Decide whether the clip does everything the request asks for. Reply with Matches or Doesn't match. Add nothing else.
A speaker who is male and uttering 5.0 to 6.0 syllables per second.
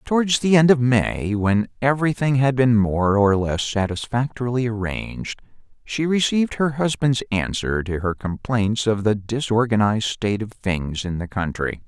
Doesn't match